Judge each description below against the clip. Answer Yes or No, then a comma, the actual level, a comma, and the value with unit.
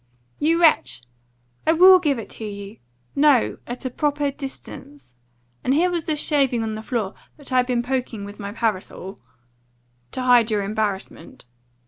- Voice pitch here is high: Yes, high, 245 Hz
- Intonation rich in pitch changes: Yes, wide, 5.9 semitones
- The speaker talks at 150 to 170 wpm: Yes, average, 165 wpm